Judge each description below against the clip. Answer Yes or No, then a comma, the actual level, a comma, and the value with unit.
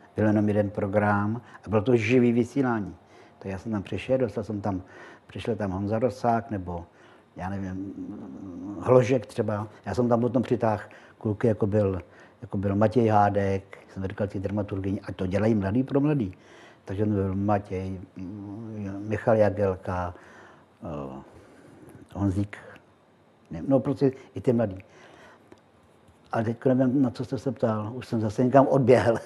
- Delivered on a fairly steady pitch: No, average, 3.3 semitones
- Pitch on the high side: No, low, 105 Hz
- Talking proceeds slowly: No, average, 150 wpm